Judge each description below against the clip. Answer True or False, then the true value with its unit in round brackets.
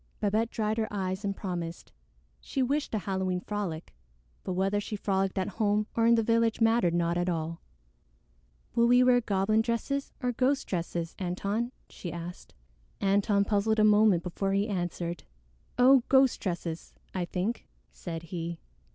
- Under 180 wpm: True (160 wpm)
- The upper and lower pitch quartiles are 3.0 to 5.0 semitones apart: True (4.2 semitones)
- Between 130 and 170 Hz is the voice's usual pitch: False (200 Hz)